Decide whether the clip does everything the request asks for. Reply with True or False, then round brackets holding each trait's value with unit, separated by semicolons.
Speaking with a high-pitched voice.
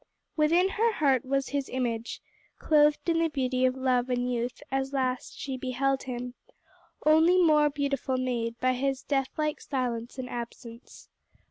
True (265 Hz)